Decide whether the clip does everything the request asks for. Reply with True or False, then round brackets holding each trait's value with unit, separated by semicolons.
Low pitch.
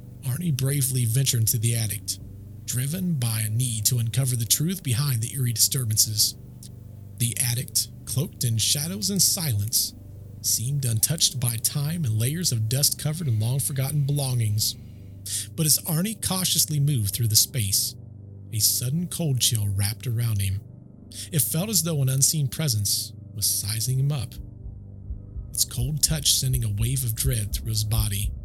True (120 Hz)